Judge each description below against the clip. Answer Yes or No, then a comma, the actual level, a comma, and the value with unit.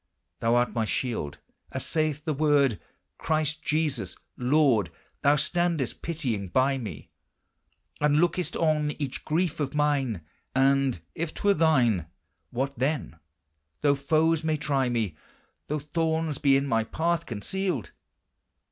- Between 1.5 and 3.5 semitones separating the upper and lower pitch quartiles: No, average, 4.1 semitones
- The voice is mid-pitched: Yes, medium, 145 Hz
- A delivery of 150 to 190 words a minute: No, slow, 135 wpm